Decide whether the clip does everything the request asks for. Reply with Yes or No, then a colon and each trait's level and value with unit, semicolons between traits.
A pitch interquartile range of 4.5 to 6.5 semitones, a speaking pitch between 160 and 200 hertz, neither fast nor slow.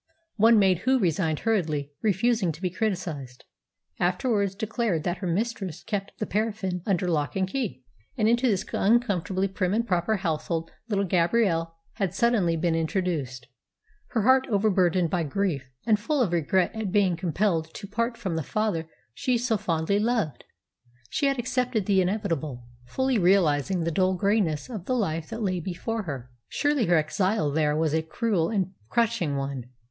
Yes: average, 5.0 semitones; high, 190 Hz; average, 165 wpm